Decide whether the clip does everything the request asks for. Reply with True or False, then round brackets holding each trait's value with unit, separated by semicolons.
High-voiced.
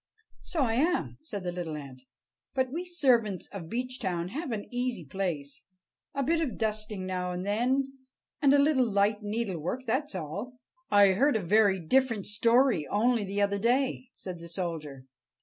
True (215 Hz)